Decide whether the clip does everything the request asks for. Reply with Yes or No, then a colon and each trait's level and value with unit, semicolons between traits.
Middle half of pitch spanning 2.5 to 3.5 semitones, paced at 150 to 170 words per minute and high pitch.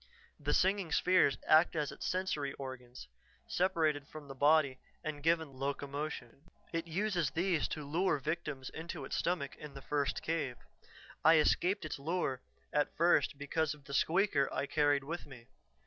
No: average, 3.1 semitones; average, 160 wpm; medium, 150 Hz